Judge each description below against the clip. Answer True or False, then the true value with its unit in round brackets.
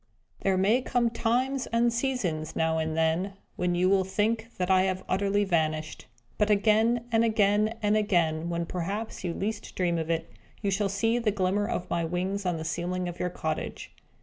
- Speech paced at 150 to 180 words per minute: False (190 wpm)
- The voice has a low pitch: False (190 Hz)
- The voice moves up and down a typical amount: True (4.0 semitones)